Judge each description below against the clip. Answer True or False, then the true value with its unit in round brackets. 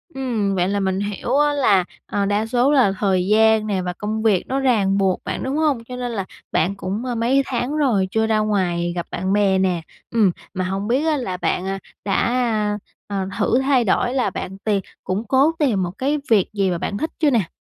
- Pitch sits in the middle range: False (210 Hz)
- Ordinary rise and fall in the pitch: True (4.6 semitones)